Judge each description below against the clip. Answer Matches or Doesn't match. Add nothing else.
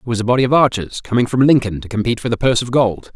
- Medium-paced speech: Doesn't match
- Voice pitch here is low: Matches